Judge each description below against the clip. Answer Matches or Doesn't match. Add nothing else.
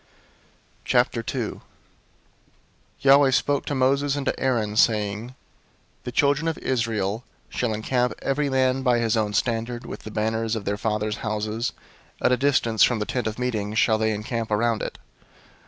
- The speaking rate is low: Doesn't match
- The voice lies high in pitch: Doesn't match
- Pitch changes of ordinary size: Matches